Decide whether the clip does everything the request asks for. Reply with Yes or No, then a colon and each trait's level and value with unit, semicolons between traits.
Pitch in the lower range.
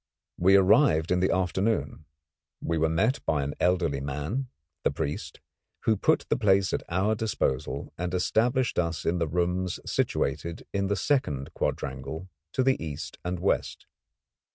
Yes: very low, 90 Hz